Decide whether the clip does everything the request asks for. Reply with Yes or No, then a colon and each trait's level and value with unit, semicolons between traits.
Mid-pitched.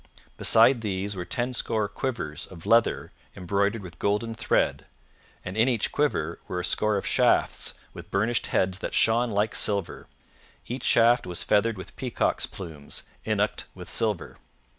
No: low, 105 Hz